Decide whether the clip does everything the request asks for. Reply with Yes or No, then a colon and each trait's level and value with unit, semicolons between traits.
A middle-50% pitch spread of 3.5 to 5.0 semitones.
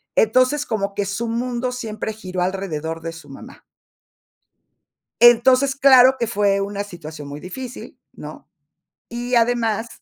Yes: average, 4.2 semitones